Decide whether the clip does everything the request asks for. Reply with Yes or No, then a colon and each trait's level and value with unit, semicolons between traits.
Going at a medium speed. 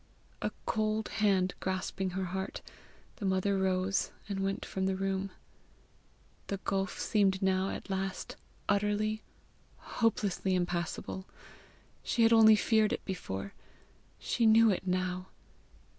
No: slow, 125 wpm